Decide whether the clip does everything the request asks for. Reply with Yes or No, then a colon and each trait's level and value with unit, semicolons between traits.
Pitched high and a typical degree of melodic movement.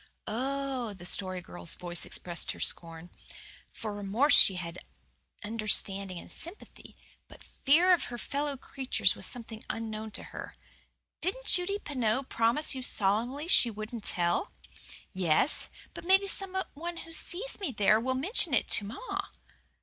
No: high, 235 Hz; wide, 7.0 semitones